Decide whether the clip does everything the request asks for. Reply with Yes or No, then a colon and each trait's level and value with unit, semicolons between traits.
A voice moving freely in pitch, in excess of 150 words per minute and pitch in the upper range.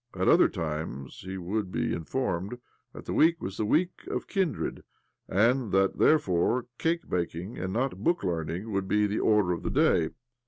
No: wide, 5.9 semitones; average, 180 wpm; low, 100 Hz